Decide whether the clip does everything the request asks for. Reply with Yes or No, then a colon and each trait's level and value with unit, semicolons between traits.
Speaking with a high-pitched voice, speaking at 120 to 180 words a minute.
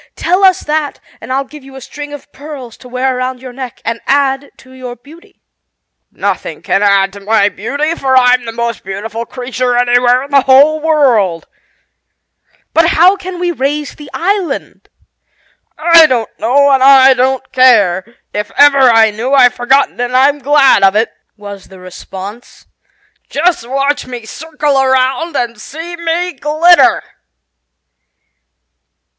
Yes: very high, 265 Hz; average, 155 wpm